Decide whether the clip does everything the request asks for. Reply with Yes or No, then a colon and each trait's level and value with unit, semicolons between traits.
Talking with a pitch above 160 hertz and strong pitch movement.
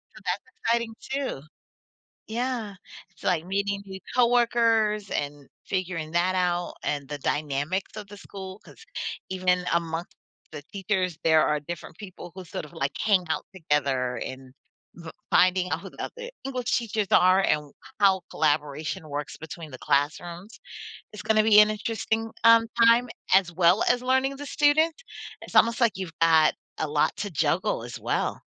Yes: medium, 185 Hz; wide, 5.9 semitones